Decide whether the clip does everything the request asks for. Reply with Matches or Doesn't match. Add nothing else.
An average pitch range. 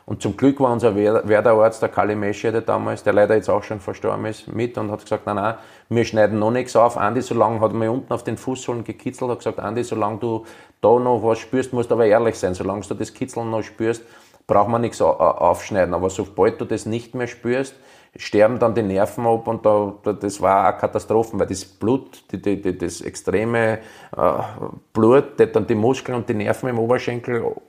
Doesn't match